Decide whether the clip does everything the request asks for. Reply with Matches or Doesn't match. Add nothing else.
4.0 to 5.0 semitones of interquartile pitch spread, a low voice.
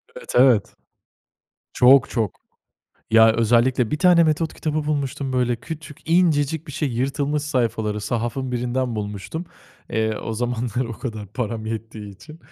Matches